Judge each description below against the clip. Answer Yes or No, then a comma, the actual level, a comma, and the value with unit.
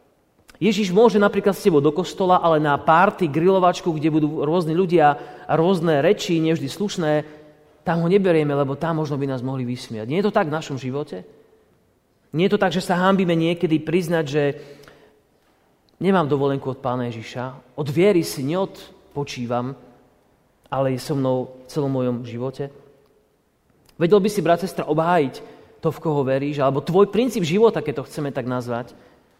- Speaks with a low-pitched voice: No, medium, 155 Hz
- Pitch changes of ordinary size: Yes, average, 4.9 semitones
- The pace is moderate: No, fast, 170 wpm